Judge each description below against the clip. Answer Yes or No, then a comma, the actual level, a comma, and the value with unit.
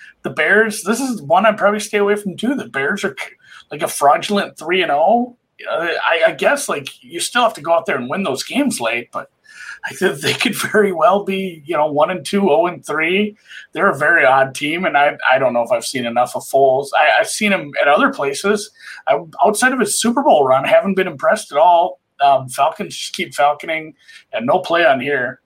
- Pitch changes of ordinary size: No, wide, 6.4 semitones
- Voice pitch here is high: Yes, high, 200 Hz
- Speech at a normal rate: No, fast, 225 wpm